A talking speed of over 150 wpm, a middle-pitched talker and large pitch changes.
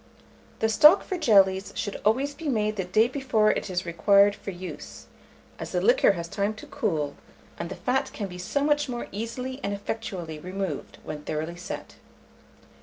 No: average, 180 wpm; high, 205 Hz; wide, 5.7 semitones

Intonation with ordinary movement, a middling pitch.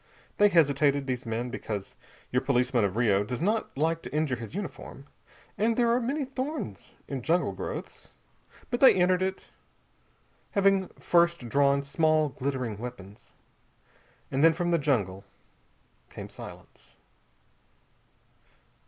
No: wide, 6.9 semitones; medium, 145 Hz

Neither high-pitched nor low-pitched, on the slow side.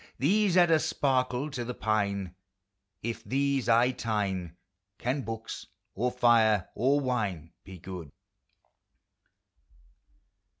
No: low, 120 Hz; slow, 110 wpm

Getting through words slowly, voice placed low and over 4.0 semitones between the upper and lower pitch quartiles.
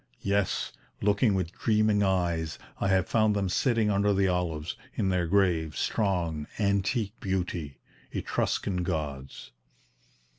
No: slow, 120 wpm; very low, 95 Hz; average, 3.1 semitones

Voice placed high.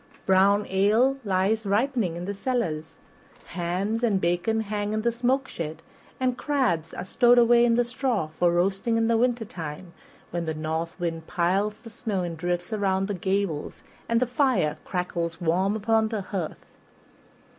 Yes: high, 200 Hz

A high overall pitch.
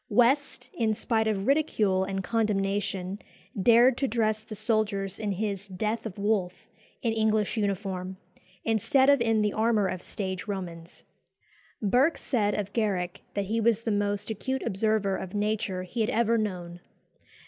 Yes: high, 210 Hz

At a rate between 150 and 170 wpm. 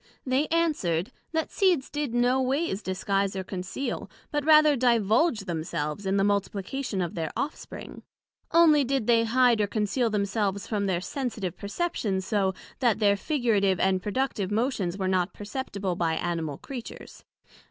Yes: average, 155 wpm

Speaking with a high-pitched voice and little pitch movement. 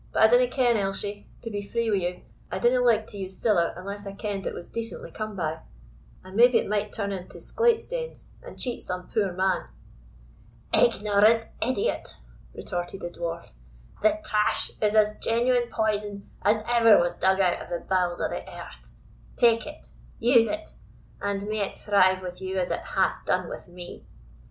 No: high, 205 Hz; average, 3.6 semitones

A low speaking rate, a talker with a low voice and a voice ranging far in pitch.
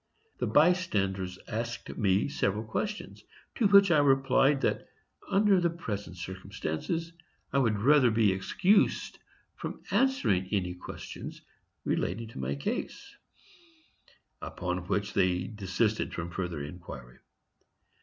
Yes: slow, 115 wpm; low, 105 Hz; wide, 8.2 semitones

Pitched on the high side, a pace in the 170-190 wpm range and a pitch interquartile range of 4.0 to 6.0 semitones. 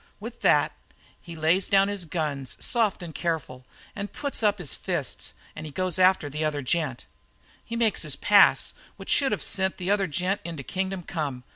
No: medium, 180 Hz; average, 180 wpm; average, 4.5 semitones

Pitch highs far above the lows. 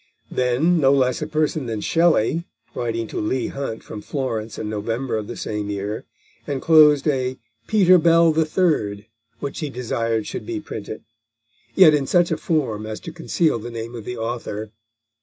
Yes: wide, 5.9 semitones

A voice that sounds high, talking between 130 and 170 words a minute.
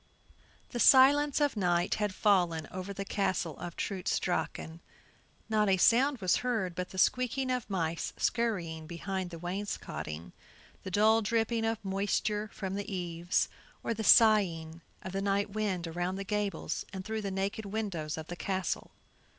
Yes: high, 195 Hz; average, 160 wpm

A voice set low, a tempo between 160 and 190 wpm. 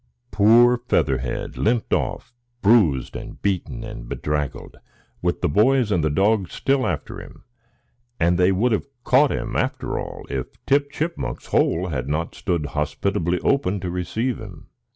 No: very low, 95 Hz; average, 150 wpm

